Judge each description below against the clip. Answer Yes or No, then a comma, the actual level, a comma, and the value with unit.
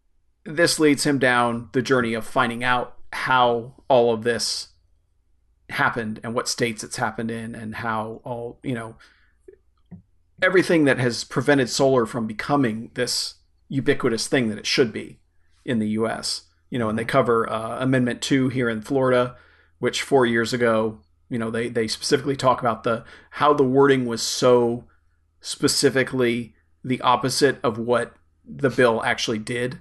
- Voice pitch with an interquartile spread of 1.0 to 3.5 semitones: Yes, average, 2.8 semitones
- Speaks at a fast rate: No, average, 160 wpm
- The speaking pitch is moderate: No, low, 120 Hz